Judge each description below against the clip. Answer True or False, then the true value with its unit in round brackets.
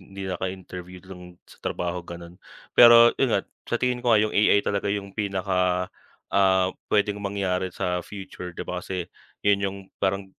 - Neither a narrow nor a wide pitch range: False (2.0 semitones)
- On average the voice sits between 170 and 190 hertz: False (95 Hz)